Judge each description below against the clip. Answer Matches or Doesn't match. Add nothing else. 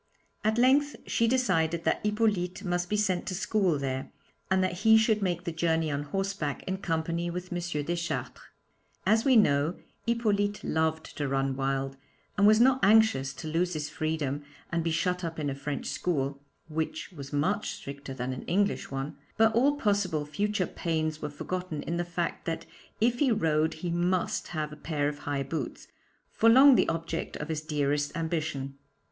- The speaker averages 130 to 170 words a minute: Doesn't match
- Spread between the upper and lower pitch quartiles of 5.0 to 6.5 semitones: Matches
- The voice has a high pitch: Doesn't match